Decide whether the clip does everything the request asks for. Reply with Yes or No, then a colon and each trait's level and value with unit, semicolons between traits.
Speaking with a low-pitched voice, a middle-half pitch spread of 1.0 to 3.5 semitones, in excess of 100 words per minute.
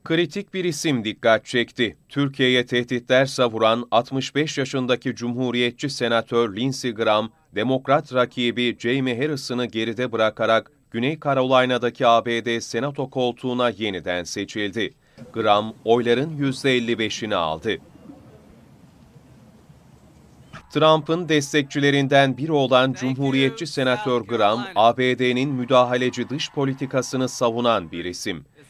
No: low, 125 Hz; average, 2.7 semitones; slow, 95 wpm